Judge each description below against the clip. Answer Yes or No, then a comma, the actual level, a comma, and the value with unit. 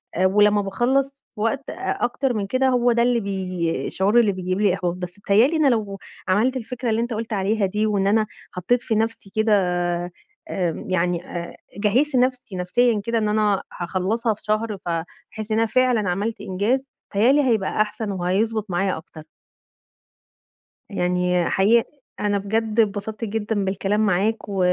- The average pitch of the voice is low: No, high, 210 Hz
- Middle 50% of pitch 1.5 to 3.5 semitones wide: Yes, average, 3.2 semitones